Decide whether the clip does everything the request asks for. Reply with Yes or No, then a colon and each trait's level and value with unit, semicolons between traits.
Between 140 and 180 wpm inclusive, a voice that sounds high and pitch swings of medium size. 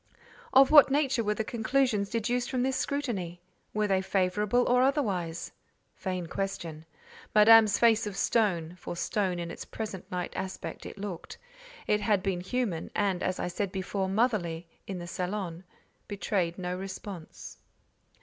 Yes: average, 155 wpm; high, 200 Hz; average, 3.8 semitones